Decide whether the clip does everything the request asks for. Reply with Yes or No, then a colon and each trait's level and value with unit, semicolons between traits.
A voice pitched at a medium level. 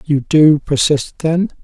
Yes: medium, 150 Hz